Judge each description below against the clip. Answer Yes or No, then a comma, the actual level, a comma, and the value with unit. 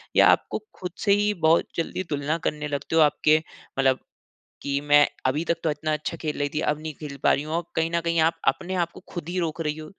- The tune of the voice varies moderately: No, narrow, 2.2 semitones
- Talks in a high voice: No, medium, 155 Hz